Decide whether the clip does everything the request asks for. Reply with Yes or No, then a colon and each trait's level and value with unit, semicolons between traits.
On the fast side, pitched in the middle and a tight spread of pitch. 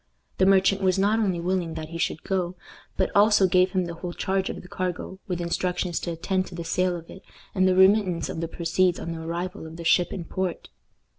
Yes: fast, 230 wpm; medium, 180 Hz; narrow, 1.9 semitones